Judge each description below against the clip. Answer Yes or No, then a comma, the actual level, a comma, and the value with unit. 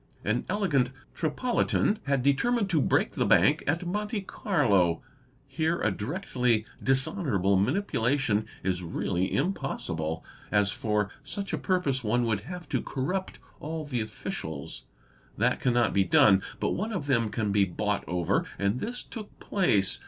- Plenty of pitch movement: Yes, wide, 9.0 semitones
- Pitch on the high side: No, low, 125 Hz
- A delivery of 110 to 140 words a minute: No, average, 150 wpm